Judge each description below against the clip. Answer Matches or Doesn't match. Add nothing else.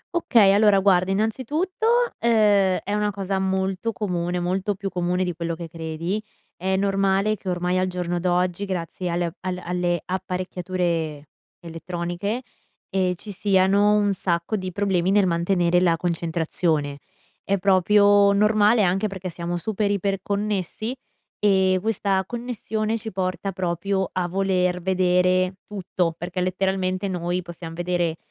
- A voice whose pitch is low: Doesn't match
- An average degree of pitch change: Doesn't match